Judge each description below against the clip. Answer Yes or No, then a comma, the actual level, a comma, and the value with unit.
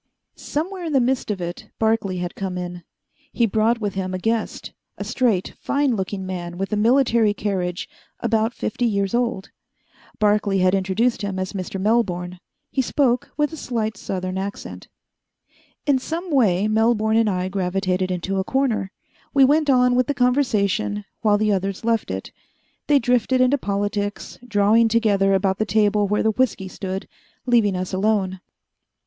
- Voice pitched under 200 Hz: No, high, 210 Hz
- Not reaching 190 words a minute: Yes, average, 165 wpm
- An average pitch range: Yes, average, 3.9 semitones